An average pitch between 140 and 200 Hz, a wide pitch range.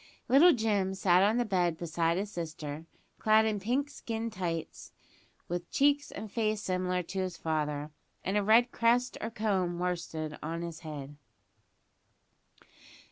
No: medium, 185 Hz; average, 4.8 semitones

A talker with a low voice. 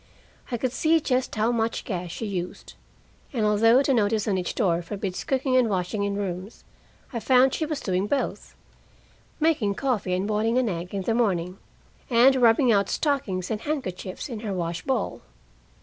No: high, 215 Hz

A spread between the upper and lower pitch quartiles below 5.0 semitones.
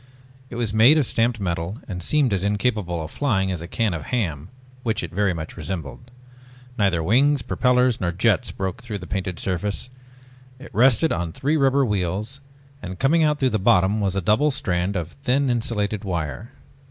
No: wide, 5.6 semitones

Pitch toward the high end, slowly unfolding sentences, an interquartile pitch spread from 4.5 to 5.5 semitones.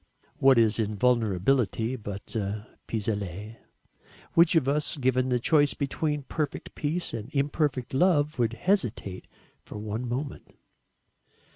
No: low, 125 Hz; slow, 125 wpm; average, 5.2 semitones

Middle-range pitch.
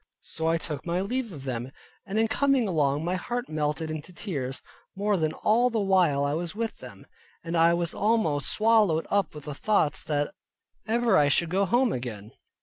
Yes: medium, 170 Hz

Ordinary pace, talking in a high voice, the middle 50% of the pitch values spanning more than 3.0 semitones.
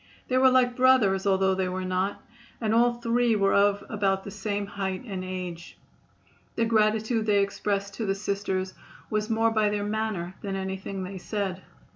No: average, 175 wpm; high, 200 Hz; narrow, 2.4 semitones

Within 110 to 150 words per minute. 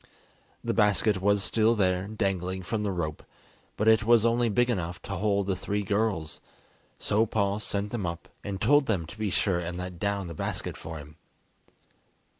No: average, 185 wpm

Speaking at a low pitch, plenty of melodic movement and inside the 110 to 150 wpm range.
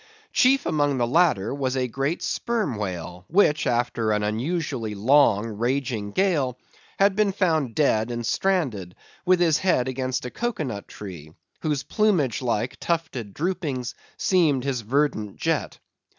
Yes: low, 130 Hz; wide, 6.6 semitones; average, 145 wpm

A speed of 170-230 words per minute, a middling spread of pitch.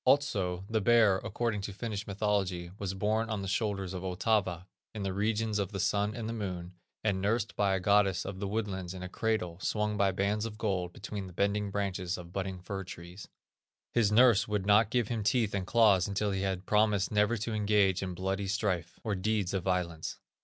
No: fast, 205 wpm; narrow, 2.2 semitones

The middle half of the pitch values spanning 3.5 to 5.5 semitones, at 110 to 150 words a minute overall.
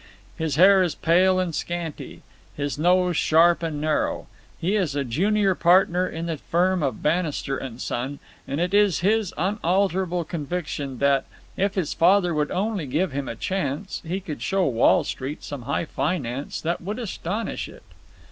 No: average, 4.3 semitones; average, 165 wpm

